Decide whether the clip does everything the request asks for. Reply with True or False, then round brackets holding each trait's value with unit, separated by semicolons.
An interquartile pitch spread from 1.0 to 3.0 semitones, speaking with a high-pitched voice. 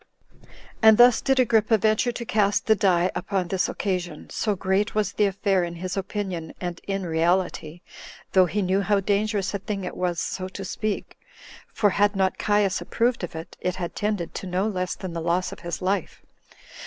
True (2.6 semitones; 195 Hz)